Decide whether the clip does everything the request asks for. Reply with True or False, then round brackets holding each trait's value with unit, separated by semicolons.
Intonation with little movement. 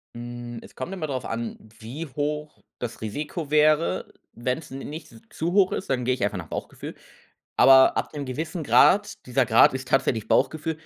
False (4.4 semitones)